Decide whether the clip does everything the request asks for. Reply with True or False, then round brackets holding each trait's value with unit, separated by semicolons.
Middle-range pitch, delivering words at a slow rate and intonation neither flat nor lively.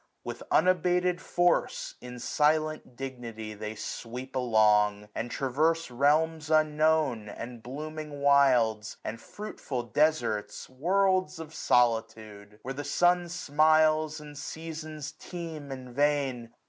True (145 Hz; 115 wpm; 4.7 semitones)